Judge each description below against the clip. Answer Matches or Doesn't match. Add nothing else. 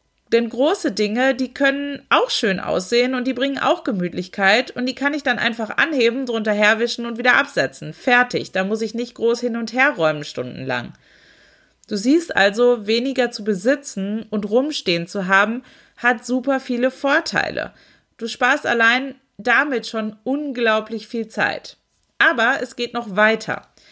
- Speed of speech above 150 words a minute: Matches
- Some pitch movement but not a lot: Matches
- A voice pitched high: Matches